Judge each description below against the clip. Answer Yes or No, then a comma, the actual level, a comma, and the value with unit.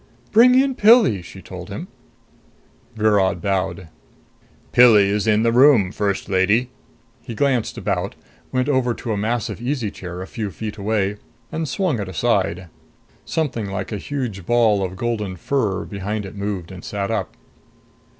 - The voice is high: No, low, 105 Hz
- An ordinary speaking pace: Yes, average, 155 wpm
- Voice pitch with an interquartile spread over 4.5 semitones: No, average, 3.9 semitones